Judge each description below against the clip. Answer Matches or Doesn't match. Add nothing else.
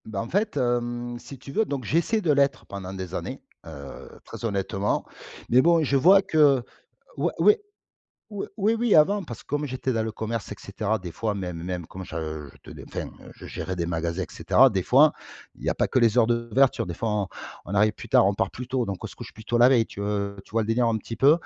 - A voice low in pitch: Matches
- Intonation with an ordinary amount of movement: Doesn't match